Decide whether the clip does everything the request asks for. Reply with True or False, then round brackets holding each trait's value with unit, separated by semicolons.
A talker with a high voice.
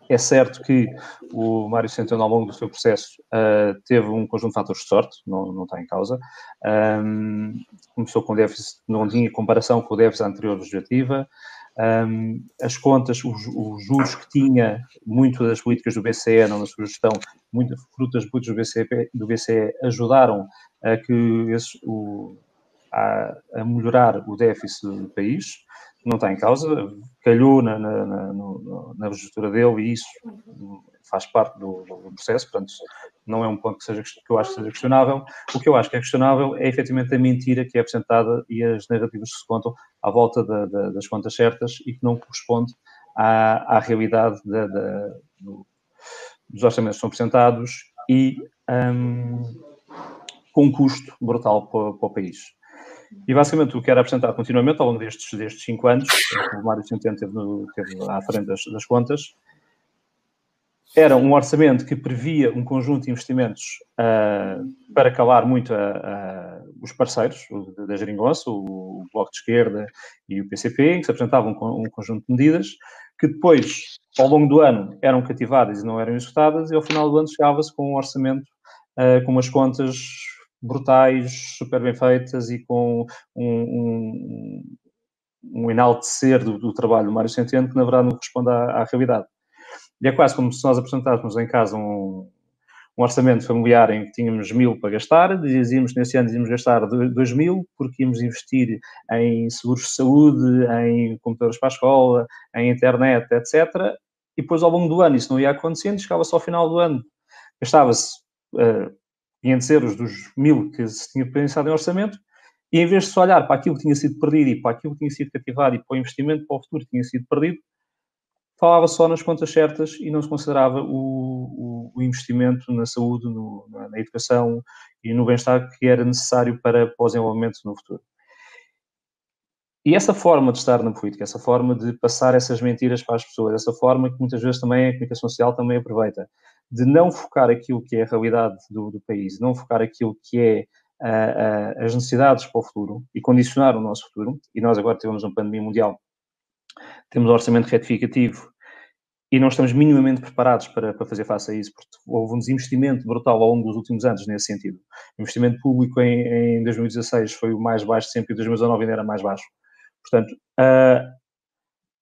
False (120 Hz)